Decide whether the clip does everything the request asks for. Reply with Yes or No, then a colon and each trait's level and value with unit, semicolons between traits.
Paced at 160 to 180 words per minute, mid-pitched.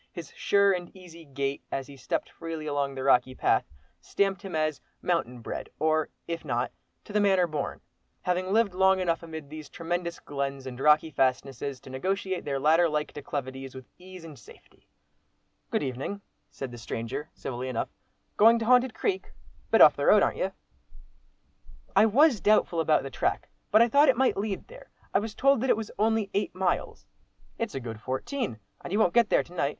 No: average, 195 wpm; medium, 165 Hz